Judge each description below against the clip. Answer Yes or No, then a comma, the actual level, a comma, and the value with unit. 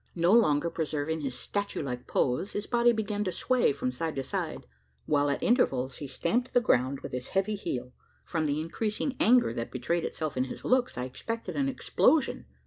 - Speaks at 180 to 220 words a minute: Yes, average, 195 wpm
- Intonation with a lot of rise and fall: Yes, wide, 8.9 semitones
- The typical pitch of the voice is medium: Yes, medium, 160 Hz